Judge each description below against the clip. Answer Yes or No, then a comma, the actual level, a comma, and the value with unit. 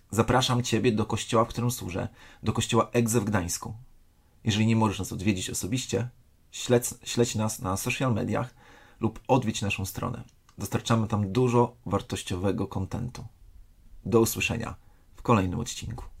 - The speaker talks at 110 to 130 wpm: No, average, 140 wpm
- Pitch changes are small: No, average, 3.6 semitones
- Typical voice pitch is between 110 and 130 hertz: Yes, low, 115 Hz